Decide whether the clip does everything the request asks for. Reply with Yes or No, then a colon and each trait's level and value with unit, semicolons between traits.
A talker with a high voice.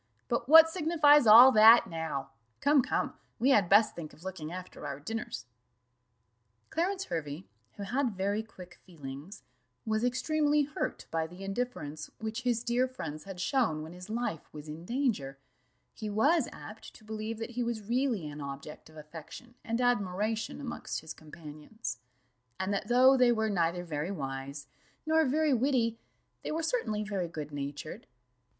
Yes: high, 215 Hz